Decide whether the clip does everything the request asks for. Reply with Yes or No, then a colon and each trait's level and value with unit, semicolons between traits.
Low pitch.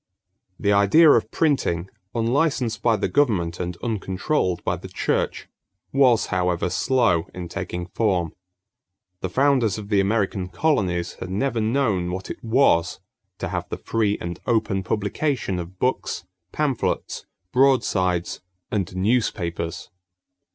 Yes: low, 100 Hz